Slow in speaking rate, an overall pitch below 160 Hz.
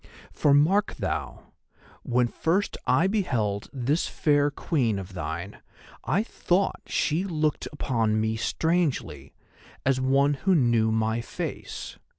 Yes: slow, 125 wpm; low, 135 Hz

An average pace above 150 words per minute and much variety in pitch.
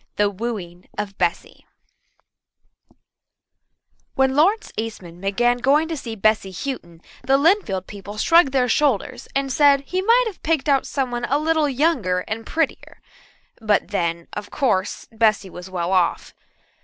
No: average, 145 wpm; wide, 6.6 semitones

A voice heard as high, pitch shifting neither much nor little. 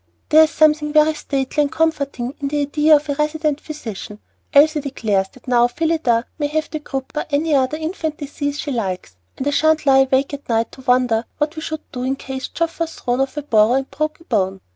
Yes: very high, 285 Hz; average, 3.3 semitones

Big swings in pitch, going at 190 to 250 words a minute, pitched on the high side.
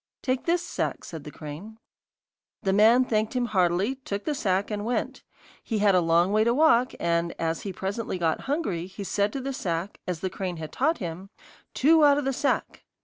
Yes: wide, 6.4 semitones; fast, 205 wpm; high, 205 Hz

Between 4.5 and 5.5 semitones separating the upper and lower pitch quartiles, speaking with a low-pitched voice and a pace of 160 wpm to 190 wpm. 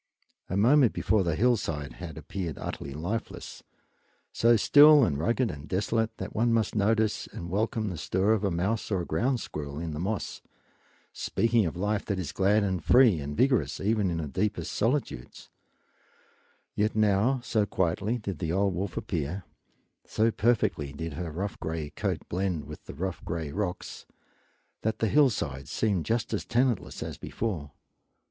Yes: average, 5.2 semitones; low, 100 Hz; average, 165 wpm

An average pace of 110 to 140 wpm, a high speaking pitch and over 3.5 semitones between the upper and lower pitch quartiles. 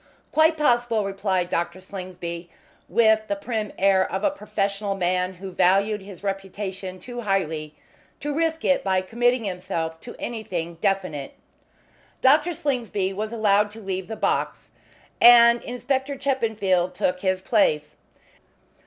Yes: slow, 135 wpm; high, 200 Hz; average, 4.3 semitones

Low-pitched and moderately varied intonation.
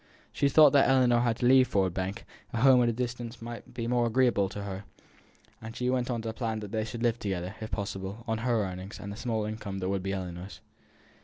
Yes: low, 115 Hz; average, 3.6 semitones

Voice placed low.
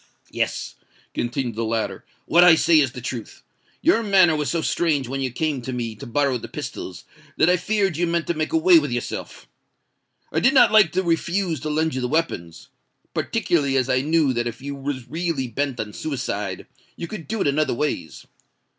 No: medium, 150 Hz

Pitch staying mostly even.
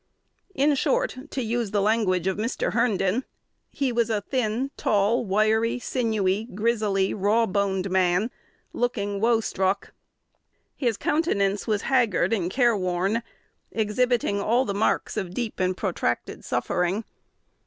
No: average, 3.5 semitones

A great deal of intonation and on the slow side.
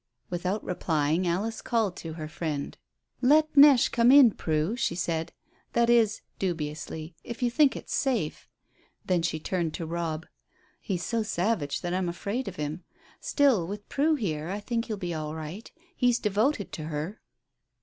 No: wide, 6.3 semitones; average, 165 wpm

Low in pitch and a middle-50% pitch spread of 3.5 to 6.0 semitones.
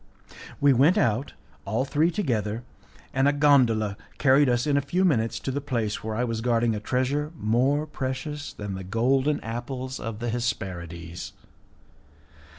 Yes: low, 125 Hz; average, 4.2 semitones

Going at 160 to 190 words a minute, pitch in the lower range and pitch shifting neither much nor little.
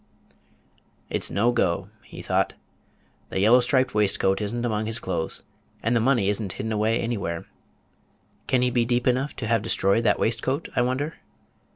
Yes: average, 175 wpm; low, 115 Hz; average, 3.0 semitones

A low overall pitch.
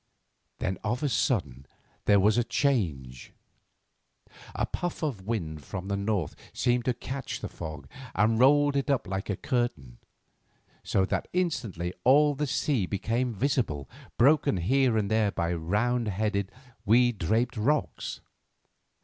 Yes: low, 110 Hz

